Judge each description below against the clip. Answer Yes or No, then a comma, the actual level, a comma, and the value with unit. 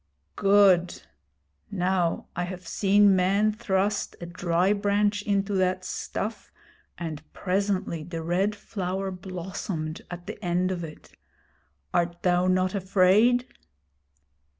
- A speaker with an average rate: No, slow, 115 wpm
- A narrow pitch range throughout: Yes, narrow, 2.2 semitones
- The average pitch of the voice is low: No, medium, 185 Hz